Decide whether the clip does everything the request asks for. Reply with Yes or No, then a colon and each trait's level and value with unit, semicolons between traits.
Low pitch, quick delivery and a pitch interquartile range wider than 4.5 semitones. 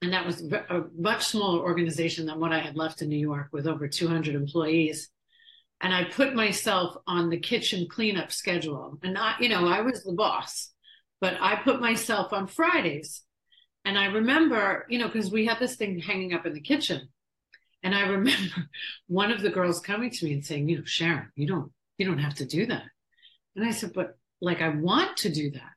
No: medium, 185 Hz; fast, 210 wpm; average, 5.0 semitones